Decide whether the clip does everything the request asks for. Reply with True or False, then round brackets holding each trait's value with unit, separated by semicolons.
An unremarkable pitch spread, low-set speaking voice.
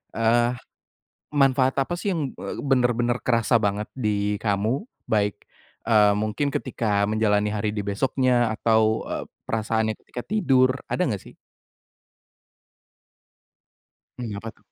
True (3.5 semitones; 115 Hz)